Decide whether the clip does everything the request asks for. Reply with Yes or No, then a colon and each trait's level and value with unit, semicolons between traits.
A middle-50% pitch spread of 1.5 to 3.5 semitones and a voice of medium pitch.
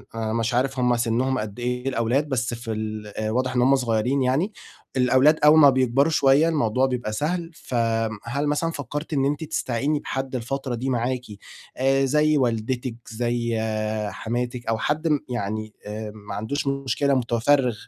No: average, 3.2 semitones; low, 125 Hz